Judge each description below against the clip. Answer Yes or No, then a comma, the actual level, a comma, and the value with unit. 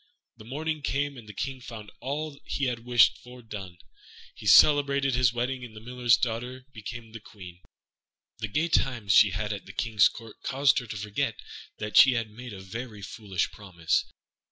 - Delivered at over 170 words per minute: Yes, average, 185 wpm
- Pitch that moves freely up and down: No, average, 3.5 semitones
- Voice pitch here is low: Yes, low, 120 Hz